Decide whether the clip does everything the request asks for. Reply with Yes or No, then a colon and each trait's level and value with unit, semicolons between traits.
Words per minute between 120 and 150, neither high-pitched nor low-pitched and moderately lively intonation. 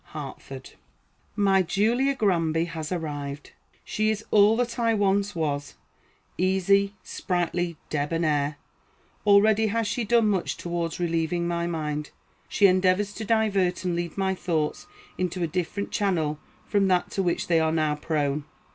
Yes: average, 145 wpm; medium, 180 Hz; average, 3.8 semitones